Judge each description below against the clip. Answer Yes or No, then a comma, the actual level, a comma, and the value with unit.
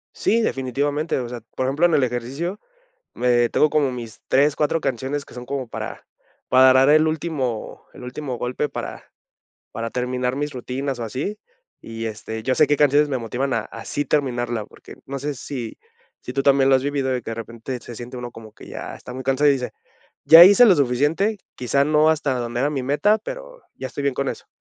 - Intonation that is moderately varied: Yes, average, 3.1 semitones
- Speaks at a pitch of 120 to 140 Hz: Yes, low, 135 Hz